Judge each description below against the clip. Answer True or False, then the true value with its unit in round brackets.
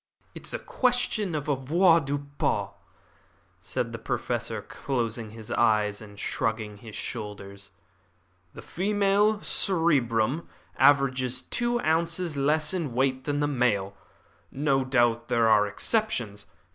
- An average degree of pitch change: False (6.7 semitones)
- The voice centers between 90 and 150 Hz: True (135 Hz)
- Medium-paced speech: False (120 wpm)